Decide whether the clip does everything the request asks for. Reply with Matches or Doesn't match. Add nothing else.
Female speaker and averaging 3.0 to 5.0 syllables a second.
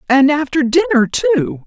Matches